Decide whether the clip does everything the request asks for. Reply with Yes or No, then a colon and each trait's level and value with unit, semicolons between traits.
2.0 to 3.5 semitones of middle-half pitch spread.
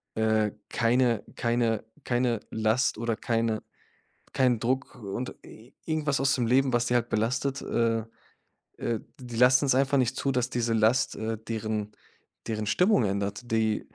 Yes: narrow, 2.6 semitones